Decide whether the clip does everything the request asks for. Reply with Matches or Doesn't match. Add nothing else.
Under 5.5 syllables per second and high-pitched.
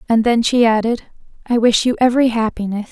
Doesn't match